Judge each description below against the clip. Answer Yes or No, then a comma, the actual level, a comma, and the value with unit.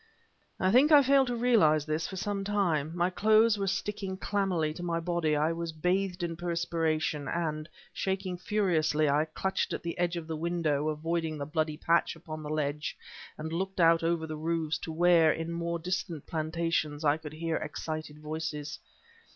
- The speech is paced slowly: No, average, 185 wpm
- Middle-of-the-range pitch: Yes, medium, 165 Hz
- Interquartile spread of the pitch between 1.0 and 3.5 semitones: Yes, average, 2.8 semitones